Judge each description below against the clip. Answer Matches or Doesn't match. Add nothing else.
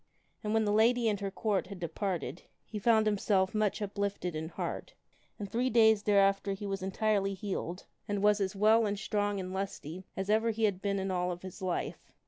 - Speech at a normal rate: Doesn't match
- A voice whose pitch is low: Doesn't match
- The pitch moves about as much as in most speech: Doesn't match